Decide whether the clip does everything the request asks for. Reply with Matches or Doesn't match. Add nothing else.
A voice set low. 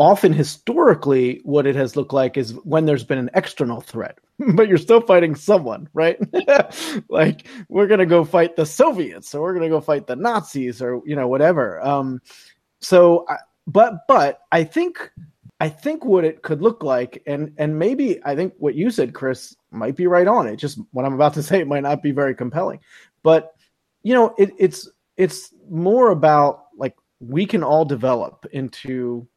Doesn't match